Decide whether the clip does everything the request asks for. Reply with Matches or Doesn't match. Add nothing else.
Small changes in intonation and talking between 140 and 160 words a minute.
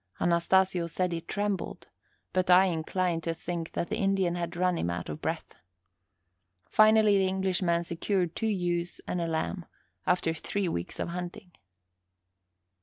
Matches